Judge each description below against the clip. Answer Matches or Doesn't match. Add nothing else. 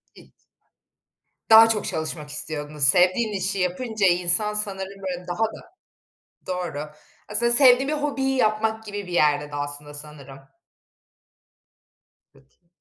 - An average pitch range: Doesn't match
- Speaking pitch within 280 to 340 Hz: Doesn't match